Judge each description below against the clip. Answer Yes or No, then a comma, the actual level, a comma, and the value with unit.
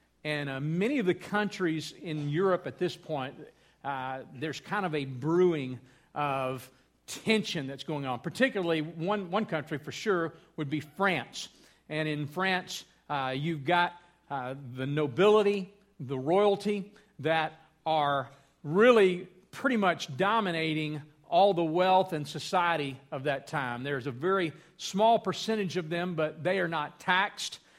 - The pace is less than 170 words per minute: Yes, average, 145 wpm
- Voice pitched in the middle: Yes, medium, 160 Hz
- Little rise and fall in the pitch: No, average, 4.4 semitones